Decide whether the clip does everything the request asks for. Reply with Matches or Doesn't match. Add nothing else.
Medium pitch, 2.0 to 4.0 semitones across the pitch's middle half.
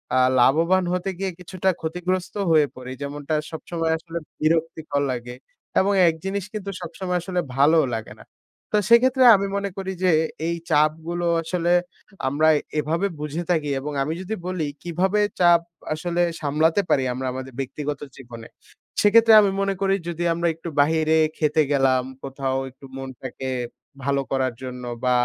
Doesn't match